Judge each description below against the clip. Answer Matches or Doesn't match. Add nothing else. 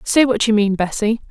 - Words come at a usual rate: Doesn't match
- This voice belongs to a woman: Matches